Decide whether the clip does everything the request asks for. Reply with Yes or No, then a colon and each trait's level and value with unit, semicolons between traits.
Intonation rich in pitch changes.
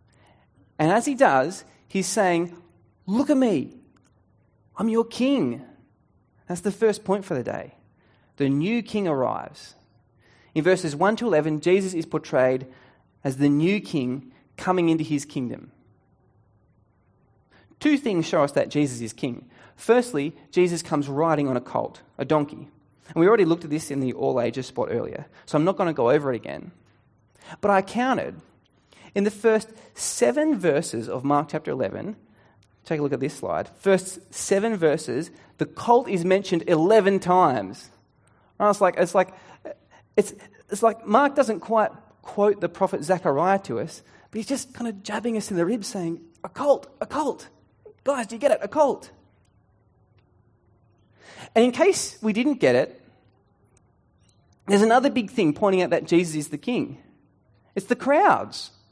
Yes: wide, 7.7 semitones